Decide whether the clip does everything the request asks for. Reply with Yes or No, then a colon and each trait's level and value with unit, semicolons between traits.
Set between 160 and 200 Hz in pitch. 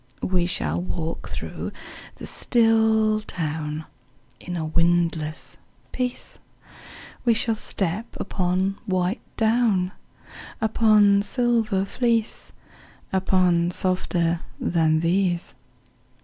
Yes: medium, 185 Hz